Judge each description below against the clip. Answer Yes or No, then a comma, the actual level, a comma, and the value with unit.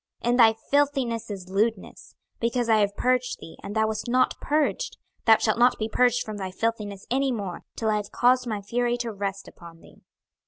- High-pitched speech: Yes, high, 225 Hz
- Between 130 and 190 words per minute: No, fast, 205 wpm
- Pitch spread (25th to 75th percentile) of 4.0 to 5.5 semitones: No, average, 3.2 semitones